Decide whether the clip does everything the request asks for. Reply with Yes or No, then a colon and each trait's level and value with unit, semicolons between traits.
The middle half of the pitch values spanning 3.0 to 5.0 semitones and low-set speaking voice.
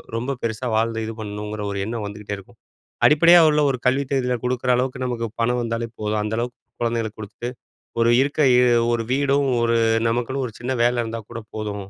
No: narrow, 2.6 semitones; low, 115 Hz